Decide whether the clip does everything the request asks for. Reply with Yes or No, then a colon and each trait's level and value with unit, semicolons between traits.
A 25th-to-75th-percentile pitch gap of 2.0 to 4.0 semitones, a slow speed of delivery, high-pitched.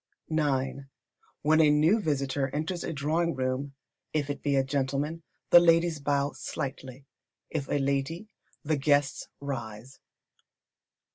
No: narrow, 2.5 semitones; slow, 130 wpm; medium, 145 Hz